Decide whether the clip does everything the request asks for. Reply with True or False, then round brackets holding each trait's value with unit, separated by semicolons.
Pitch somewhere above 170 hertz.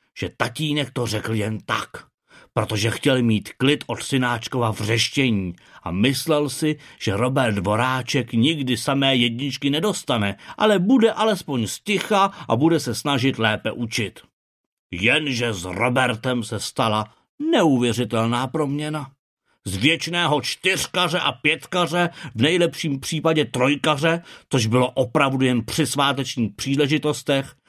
False (135 Hz)